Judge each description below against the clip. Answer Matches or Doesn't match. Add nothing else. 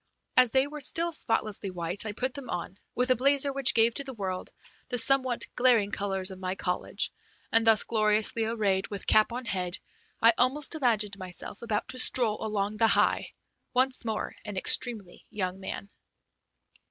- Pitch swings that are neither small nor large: Matches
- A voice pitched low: Doesn't match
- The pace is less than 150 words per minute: Doesn't match